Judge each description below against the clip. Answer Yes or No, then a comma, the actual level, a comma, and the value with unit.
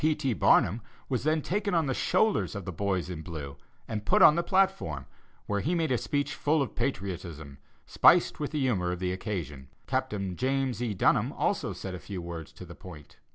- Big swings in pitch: Yes, wide, 8.3 semitones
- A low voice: Yes, low, 105 Hz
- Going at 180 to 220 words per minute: Yes, fast, 205 wpm